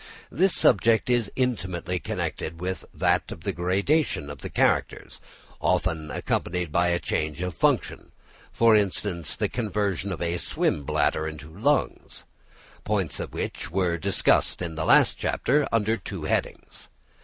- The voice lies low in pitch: Yes, very low, 90 Hz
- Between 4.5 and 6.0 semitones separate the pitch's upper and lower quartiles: Yes, average, 4.9 semitones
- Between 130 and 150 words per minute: Yes, average, 145 wpm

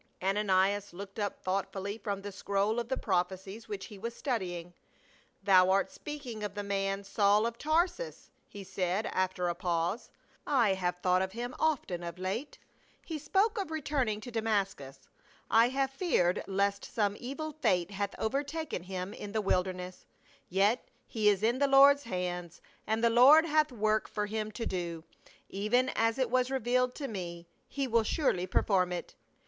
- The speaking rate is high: No, average, 175 wpm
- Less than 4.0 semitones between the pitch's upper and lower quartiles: No, average, 4.8 semitones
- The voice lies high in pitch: Yes, high, 205 Hz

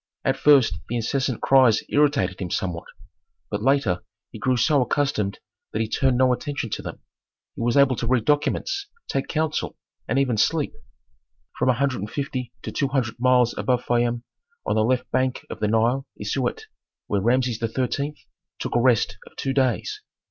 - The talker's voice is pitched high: No, low, 125 Hz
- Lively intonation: No, average, 3.1 semitones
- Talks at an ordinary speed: Yes, average, 180 wpm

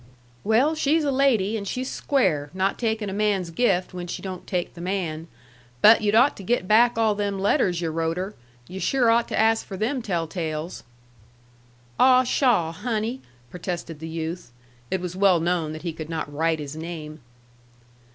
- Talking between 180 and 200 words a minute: Yes, average, 190 wpm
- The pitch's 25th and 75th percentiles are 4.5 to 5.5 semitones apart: Yes, average, 5.2 semitones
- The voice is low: No, high, 190 Hz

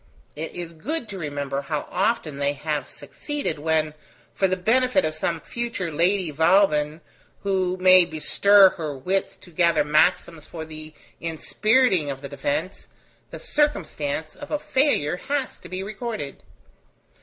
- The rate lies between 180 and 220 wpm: No, average, 145 wpm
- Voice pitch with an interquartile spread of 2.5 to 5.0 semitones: Yes, average, 4.7 semitones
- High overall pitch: No, medium, 170 Hz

